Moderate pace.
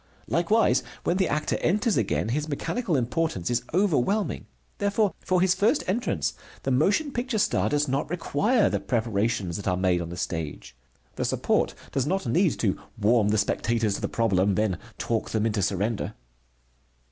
Yes: average, 170 wpm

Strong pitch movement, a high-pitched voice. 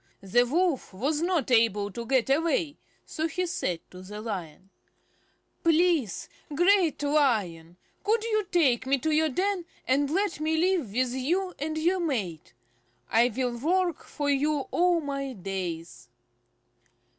Yes: wide, 7.1 semitones; very high, 285 Hz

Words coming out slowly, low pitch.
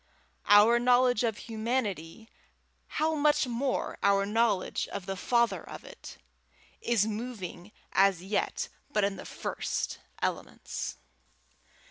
No: slow, 115 wpm; high, 220 Hz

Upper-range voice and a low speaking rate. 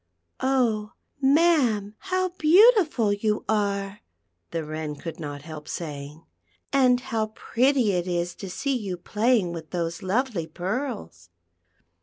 Yes: high, 205 Hz; slow, 125 wpm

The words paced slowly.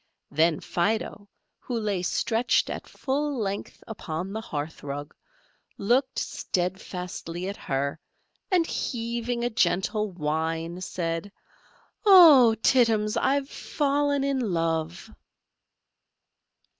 Yes: slow, 100 wpm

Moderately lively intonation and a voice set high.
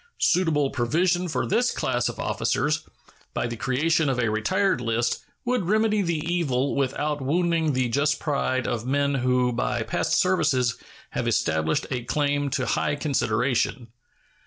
No: average, 4.8 semitones; medium, 140 Hz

